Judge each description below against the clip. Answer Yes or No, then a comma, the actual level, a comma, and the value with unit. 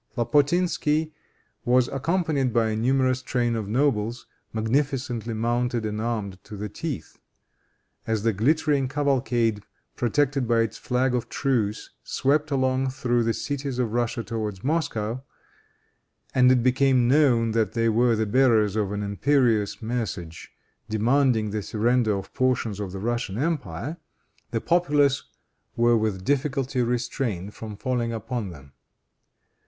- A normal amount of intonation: Yes, average, 3.5 semitones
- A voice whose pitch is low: Yes, low, 120 Hz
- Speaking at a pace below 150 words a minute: Yes, slow, 135 wpm